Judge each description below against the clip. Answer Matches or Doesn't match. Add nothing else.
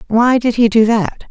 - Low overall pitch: Doesn't match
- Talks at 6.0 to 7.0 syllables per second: Doesn't match